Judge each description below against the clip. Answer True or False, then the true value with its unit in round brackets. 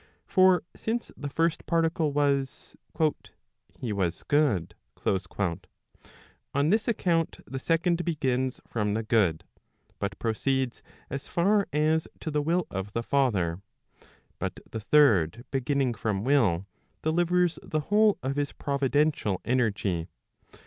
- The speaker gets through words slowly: True (125 wpm)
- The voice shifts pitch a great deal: True (7.2 semitones)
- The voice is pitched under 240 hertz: True (135 Hz)